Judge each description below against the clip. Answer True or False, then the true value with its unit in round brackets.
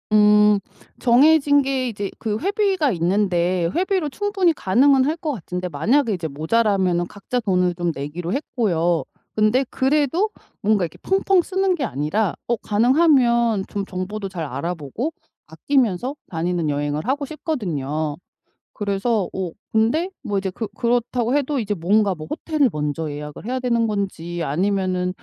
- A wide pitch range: True (7.2 semitones)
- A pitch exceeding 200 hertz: True (210 Hz)